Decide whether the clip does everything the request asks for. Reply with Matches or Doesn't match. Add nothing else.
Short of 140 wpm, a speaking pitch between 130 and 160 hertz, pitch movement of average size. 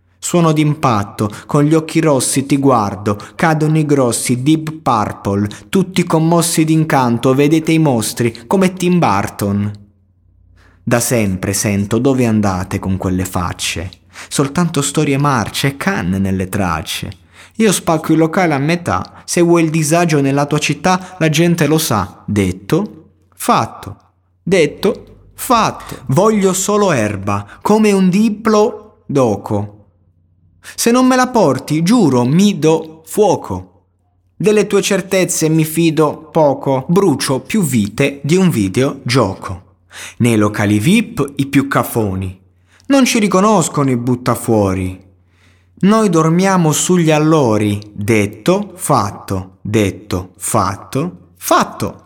Doesn't match